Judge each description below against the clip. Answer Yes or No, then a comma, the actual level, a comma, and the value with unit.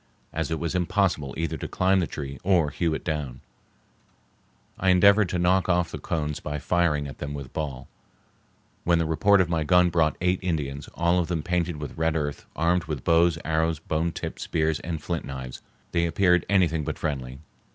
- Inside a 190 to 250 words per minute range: Yes, average, 195 wpm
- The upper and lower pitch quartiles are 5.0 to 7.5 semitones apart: No, average, 2.8 semitones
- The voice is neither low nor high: No, very low, 80 Hz